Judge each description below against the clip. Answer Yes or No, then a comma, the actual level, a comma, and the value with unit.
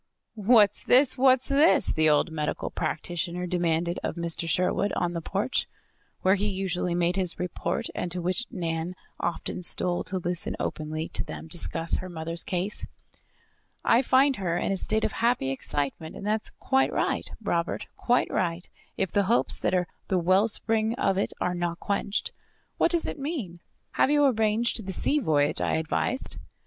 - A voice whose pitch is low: No, medium, 185 Hz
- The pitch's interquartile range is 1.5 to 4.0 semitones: No, average, 4.5 semitones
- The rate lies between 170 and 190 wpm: Yes, average, 175 wpm